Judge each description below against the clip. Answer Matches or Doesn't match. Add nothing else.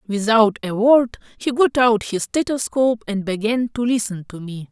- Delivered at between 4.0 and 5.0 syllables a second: Matches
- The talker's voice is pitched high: Matches